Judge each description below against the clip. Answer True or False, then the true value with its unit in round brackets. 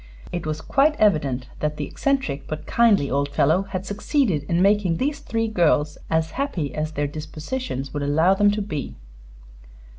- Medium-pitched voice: True (165 Hz)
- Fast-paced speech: False (170 wpm)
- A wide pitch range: True (5.9 semitones)